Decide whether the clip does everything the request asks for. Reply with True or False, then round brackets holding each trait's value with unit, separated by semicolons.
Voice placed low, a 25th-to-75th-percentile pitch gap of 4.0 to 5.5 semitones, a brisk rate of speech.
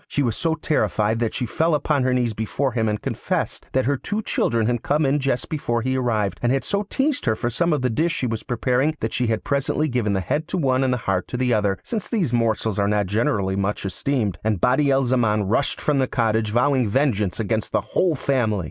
True (125 Hz; 4.4 semitones; 240 wpm)